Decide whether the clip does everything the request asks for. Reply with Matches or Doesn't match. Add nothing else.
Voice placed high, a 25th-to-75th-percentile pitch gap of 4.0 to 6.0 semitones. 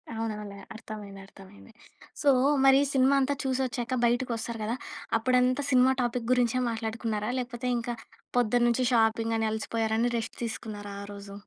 Doesn't match